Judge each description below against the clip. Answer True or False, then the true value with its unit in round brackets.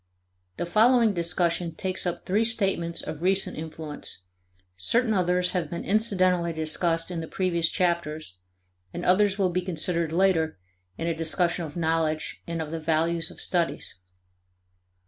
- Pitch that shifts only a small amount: True (2.3 semitones)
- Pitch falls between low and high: True (170 Hz)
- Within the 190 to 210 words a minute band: False (145 wpm)